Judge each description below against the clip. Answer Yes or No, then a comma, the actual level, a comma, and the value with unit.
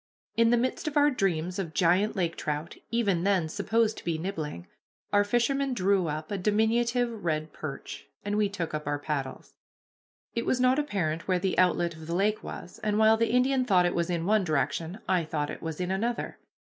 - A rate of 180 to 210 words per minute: Yes, fast, 205 wpm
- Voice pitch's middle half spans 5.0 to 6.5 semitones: Yes, wide, 5.6 semitones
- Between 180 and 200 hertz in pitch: Yes, high, 190 Hz